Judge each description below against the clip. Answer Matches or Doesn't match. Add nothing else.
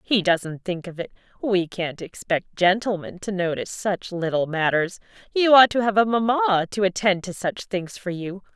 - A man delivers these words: Doesn't match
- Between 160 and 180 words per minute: Doesn't match